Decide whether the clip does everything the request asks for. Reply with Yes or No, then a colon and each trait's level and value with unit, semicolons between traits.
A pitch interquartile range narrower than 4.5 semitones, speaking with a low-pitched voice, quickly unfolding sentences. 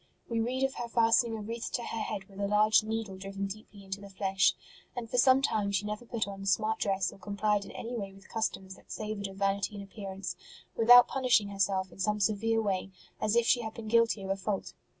No: narrow, 2.5 semitones; high, 210 Hz; fast, 235 wpm